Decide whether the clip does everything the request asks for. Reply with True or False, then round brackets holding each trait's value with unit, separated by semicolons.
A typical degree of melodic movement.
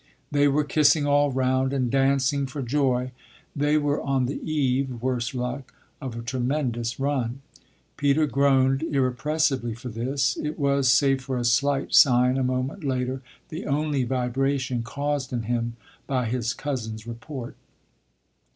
False (2.3 semitones)